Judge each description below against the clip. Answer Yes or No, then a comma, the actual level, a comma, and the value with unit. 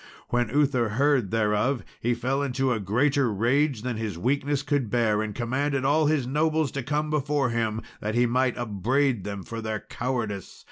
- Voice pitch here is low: Yes, low, 125 Hz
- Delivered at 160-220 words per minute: Yes, average, 180 wpm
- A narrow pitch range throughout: No, average, 4.2 semitones